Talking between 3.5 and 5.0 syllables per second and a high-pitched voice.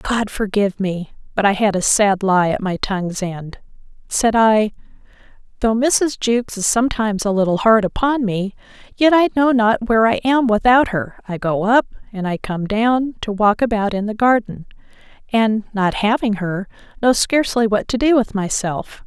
Yes: 4.3 syllables/s; high, 215 Hz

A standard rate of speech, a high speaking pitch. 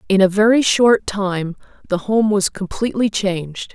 Yes: average, 160 wpm; high, 200 Hz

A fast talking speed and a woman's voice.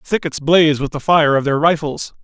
No: fast, 240 wpm; male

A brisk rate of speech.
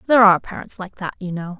Yes: fast, 265 wpm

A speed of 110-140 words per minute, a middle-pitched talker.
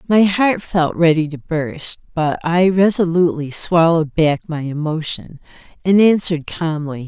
Yes: slow, 135 wpm; medium, 165 Hz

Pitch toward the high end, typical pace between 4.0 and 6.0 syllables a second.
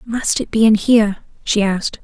Yes: high, 215 Hz; 5.3 syllables/s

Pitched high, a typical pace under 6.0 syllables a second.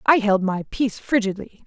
Yes: high, 215 Hz; 5.4 syllables/s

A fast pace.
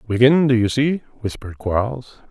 No: average, 155 wpm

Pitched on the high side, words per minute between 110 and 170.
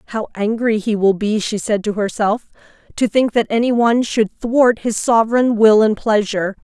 No: high, 220 Hz; average, 190 wpm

